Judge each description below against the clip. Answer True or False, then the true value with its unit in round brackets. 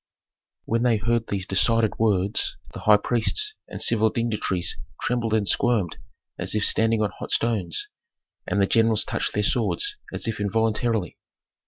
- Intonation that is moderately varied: False (2.2 semitones)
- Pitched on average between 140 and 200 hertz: False (110 Hz)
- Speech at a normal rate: True (155 wpm)